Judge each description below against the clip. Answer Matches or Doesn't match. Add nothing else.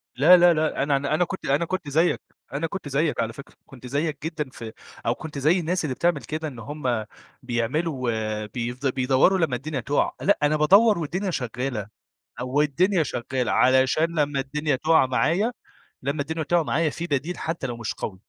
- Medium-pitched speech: Matches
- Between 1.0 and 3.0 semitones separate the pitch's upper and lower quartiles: Doesn't match